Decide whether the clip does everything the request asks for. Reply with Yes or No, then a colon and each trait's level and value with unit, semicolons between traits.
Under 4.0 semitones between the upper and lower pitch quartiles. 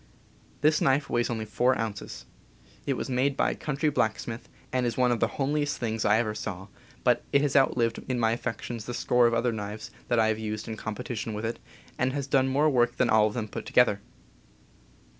Yes: average, 3.0 semitones